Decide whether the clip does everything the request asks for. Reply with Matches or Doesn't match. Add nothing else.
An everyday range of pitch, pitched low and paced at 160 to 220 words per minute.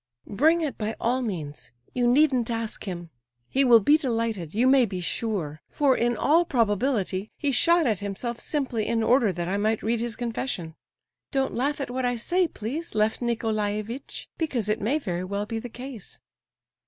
Doesn't match